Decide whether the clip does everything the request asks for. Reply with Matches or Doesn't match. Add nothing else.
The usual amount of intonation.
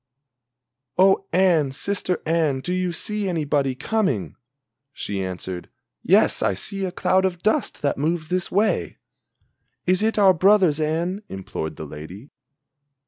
Doesn't match